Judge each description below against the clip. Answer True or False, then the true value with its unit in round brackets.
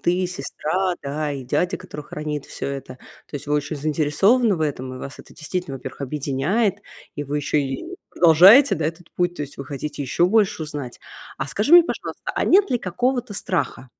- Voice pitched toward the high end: False (155 Hz)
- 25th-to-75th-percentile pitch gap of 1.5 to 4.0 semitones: False (4.7 semitones)